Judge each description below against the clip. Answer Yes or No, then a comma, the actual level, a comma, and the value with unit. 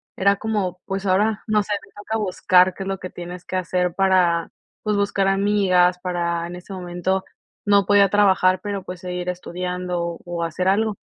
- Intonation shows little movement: Yes, narrow, 1.9 semitones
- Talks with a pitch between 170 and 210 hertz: Yes, medium, 185 Hz